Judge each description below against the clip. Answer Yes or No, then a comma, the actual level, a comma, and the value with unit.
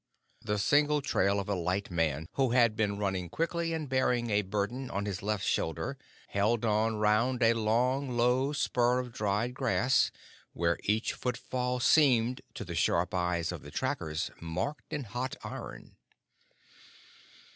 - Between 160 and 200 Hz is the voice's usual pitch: No, low, 115 Hz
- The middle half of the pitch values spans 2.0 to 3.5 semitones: No, average, 4.2 semitones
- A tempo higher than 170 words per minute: No, average, 155 wpm